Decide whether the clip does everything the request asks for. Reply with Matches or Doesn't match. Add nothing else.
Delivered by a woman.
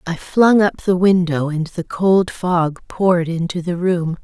Matches